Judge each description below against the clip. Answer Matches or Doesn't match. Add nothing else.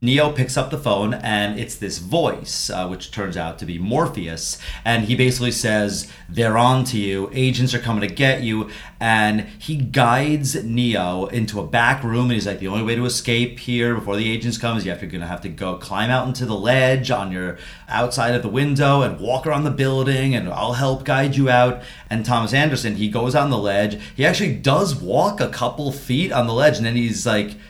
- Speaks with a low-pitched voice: Matches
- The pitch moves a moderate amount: Matches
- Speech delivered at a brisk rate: Matches